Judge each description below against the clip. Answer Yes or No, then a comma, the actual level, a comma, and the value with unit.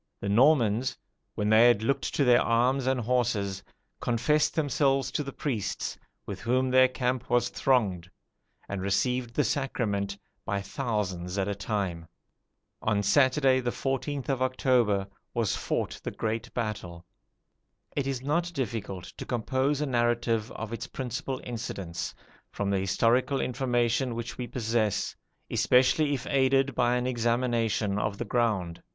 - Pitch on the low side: Yes, low, 120 Hz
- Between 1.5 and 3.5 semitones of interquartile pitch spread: No, average, 3.9 semitones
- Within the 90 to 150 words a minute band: Yes, average, 145 wpm